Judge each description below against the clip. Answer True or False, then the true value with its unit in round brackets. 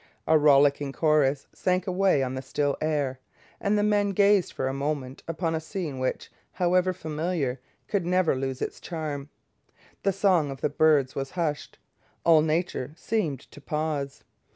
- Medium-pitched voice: True (155 Hz)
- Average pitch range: True (4.6 semitones)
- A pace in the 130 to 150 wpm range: False (160 wpm)